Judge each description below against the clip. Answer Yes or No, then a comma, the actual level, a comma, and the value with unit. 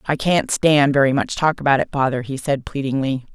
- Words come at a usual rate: No, fast, 215 wpm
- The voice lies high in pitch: No, medium, 140 Hz